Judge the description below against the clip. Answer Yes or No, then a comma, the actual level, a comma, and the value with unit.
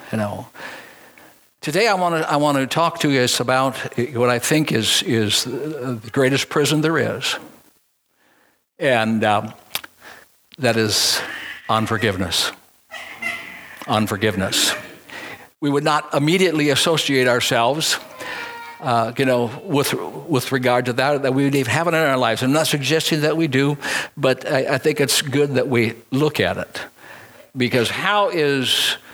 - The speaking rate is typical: Yes, average, 150 wpm